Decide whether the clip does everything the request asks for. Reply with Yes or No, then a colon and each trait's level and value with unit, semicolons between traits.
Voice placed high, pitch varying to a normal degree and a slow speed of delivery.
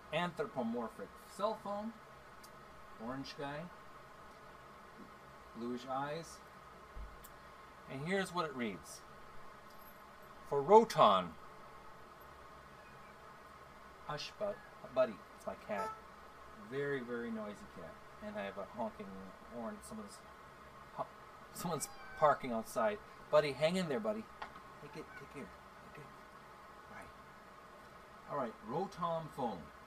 No: high, 210 Hz; narrow, 0.2 semitones; slow, 100 wpm